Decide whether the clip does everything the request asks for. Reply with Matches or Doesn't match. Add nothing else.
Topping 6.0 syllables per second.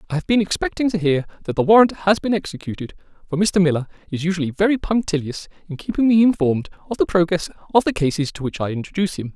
Matches